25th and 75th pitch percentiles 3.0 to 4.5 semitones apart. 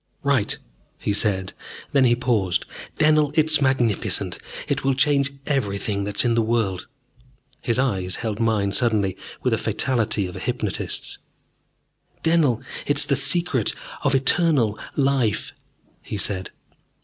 No: average, 5.2 semitones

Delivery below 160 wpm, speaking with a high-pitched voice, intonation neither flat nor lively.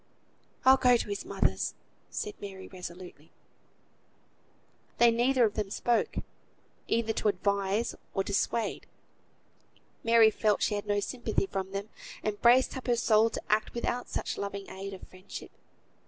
Yes: average, 145 wpm; high, 215 Hz; average, 3.1 semitones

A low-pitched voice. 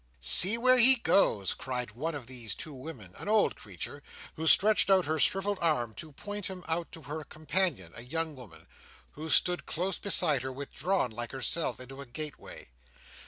No: medium, 155 Hz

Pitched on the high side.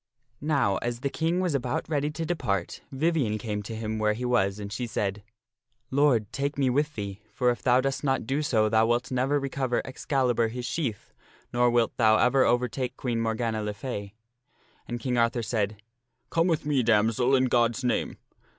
No: low, 120 Hz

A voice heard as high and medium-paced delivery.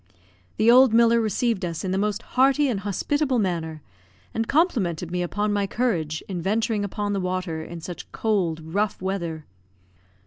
Yes: high, 200 Hz; average, 165 wpm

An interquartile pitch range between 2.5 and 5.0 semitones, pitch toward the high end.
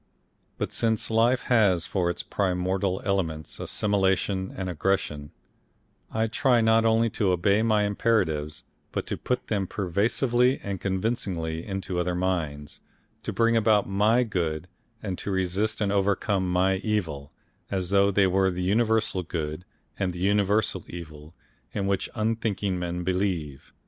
No: average, 3.3 semitones; very low, 95 Hz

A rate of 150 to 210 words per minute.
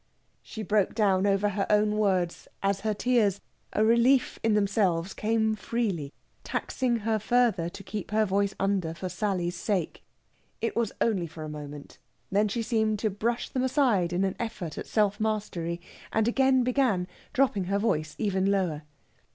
Yes: average, 170 wpm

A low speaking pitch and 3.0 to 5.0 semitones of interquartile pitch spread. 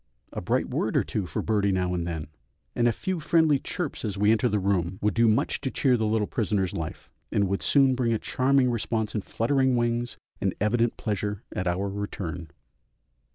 Yes: low, 105 Hz; average, 3.9 semitones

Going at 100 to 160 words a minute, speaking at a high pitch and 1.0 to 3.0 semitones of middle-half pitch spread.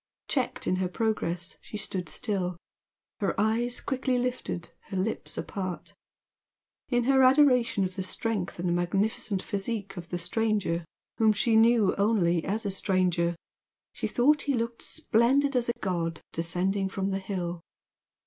No: average, 150 wpm; high, 200 Hz; average, 4.5 semitones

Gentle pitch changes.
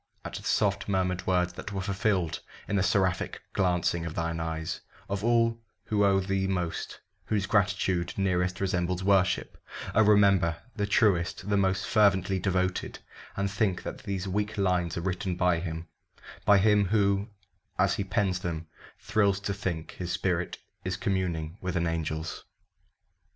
Yes: narrow, 2.1 semitones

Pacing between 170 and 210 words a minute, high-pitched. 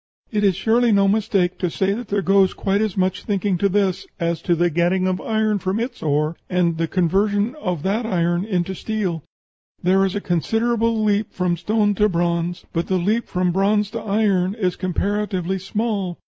Yes: average, 190 wpm; high, 195 Hz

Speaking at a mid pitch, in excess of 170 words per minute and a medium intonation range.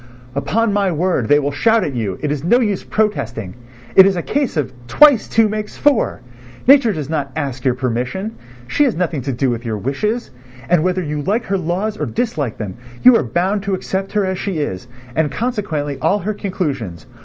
No: medium, 175 Hz; fast, 205 wpm; wide, 7.4 semitones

